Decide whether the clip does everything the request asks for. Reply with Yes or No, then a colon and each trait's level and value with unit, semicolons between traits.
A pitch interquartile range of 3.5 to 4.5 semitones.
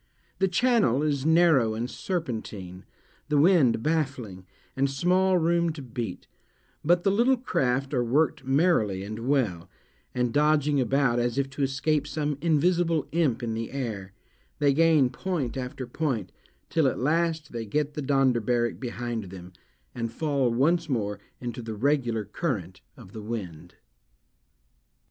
No: average, 5.2 semitones